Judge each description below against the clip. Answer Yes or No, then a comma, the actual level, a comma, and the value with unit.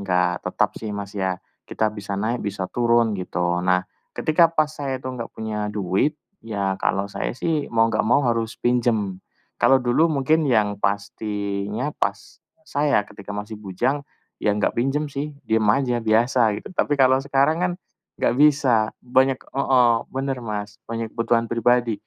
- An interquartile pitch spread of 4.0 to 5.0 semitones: Yes, average, 4.5 semitones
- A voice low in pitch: Yes, low, 115 Hz